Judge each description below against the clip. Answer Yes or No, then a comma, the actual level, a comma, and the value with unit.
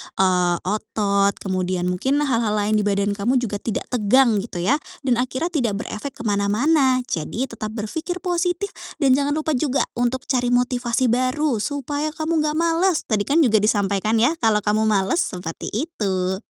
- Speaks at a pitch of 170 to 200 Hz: No, high, 240 Hz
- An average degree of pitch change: No, wide, 5.8 semitones